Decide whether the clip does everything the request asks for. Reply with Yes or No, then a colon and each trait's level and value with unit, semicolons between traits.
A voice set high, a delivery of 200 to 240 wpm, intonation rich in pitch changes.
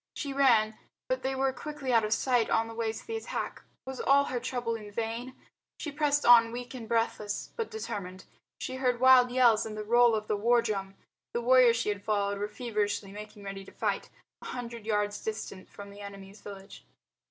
No: high, 230 Hz; fast, 205 wpm; average, 3.5 semitones